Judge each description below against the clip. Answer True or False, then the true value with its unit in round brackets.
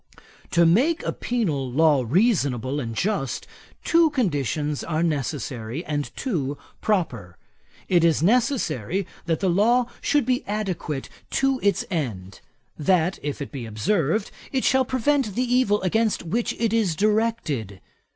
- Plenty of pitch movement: True (8.2 semitones)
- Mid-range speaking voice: True (175 Hz)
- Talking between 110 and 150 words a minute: True (140 wpm)